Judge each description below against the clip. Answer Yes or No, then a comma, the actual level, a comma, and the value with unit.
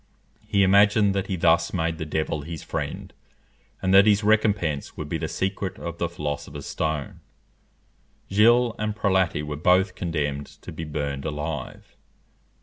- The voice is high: No, very low, 85 Hz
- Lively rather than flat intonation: No, average, 4.6 semitones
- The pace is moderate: Yes, average, 150 wpm